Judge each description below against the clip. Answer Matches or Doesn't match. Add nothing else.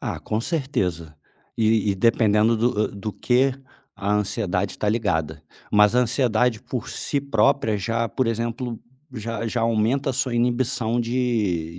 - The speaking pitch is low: Matches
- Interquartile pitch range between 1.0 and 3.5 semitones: Matches